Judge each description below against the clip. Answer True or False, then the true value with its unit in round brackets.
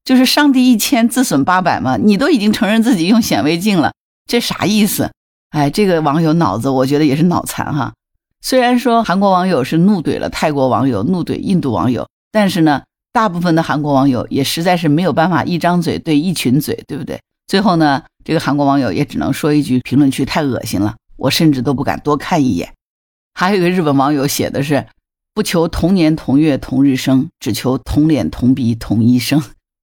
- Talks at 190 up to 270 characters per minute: False (310 characters per minute)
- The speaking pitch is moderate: True (155 Hz)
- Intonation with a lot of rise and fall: True (5.8 semitones)